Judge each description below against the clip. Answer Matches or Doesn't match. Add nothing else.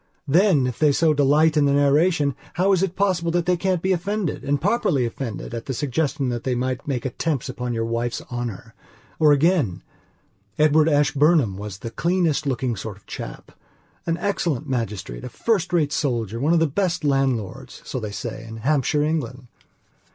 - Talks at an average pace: Matches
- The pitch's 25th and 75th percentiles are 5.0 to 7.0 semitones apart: Matches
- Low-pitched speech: Doesn't match